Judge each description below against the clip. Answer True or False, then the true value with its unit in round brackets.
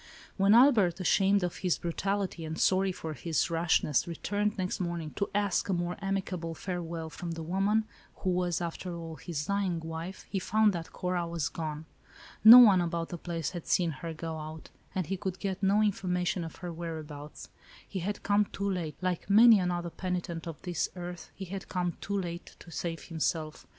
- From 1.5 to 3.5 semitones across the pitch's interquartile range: True (2.8 semitones)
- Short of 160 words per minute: False (190 wpm)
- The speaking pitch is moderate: True (175 Hz)